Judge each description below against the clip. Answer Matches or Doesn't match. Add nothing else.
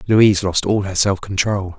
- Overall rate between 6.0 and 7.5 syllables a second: Doesn't match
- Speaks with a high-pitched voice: Doesn't match